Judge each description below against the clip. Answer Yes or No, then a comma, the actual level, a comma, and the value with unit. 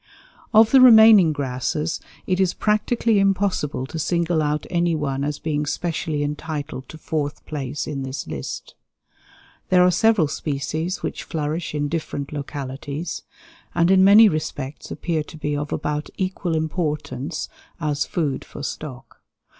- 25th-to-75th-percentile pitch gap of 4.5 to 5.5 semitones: No, average, 3.5 semitones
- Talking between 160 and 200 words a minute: No, average, 145 wpm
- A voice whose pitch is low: No, medium, 155 Hz